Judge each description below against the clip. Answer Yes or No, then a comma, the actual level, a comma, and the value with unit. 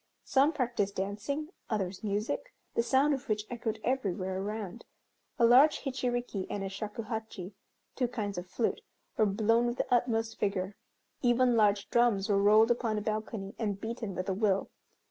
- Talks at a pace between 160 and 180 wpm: Yes, average, 165 wpm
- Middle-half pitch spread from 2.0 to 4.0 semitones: Yes, average, 3.2 semitones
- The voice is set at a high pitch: Yes, high, 220 Hz